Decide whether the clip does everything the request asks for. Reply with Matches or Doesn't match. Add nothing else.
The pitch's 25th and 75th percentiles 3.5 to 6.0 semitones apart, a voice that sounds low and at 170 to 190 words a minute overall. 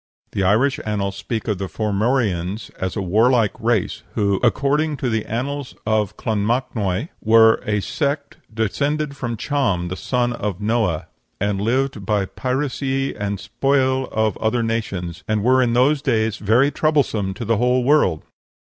Doesn't match